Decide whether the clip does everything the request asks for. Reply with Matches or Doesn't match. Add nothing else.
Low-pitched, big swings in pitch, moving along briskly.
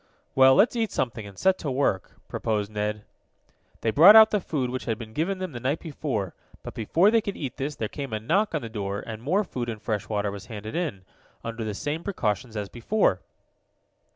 Matches